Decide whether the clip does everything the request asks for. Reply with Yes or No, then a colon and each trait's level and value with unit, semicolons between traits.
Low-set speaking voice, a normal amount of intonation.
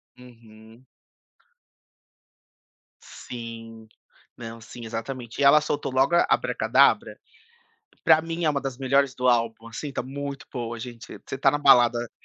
Yes: low, 125 Hz; average, 3.2 semitones